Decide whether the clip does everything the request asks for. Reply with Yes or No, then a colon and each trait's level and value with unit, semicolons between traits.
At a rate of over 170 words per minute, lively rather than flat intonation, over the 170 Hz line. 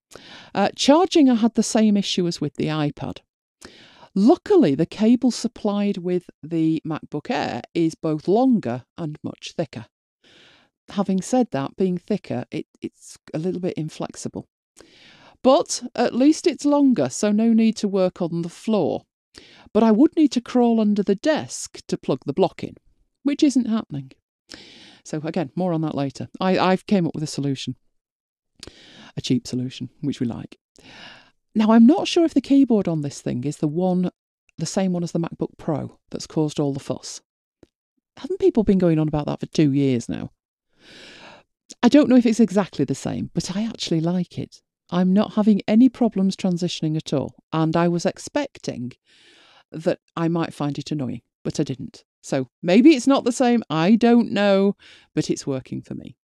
Yes: average, 180 wpm; wide, 7.0 semitones; medium, 185 Hz